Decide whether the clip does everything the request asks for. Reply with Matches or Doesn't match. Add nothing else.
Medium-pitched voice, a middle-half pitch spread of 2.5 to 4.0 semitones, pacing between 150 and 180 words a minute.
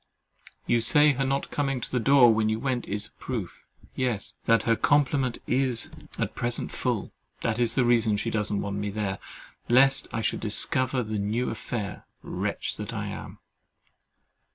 Doesn't match